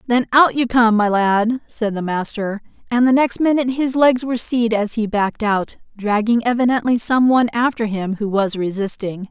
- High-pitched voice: Yes, high, 230 Hz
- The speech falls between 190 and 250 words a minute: Yes, average, 195 wpm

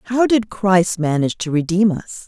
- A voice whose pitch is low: No, high, 190 Hz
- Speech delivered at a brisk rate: No, average, 185 wpm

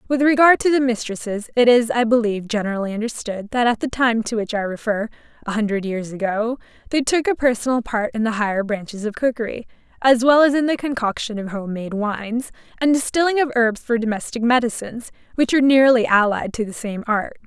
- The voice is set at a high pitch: Yes, high, 230 Hz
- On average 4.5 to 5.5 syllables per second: No, 5.9 syllables/s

